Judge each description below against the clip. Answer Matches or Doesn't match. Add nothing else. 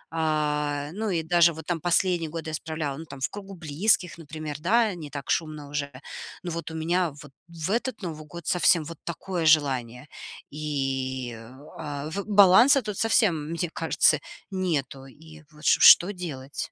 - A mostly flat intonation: Doesn't match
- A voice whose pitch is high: Doesn't match